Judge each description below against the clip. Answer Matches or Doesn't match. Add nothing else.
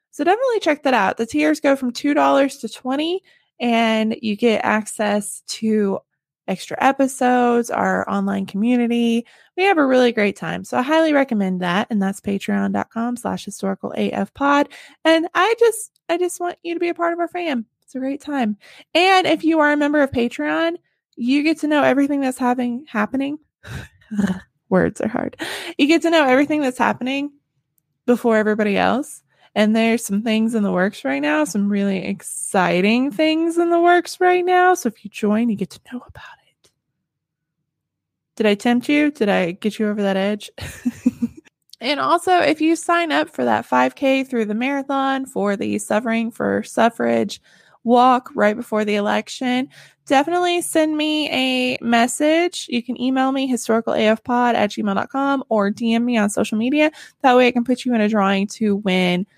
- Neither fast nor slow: Matches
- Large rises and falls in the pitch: Matches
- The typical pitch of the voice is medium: Doesn't match